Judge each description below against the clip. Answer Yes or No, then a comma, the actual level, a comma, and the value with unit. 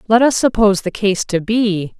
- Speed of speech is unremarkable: No, fast, 210 wpm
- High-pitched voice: Yes, high, 205 Hz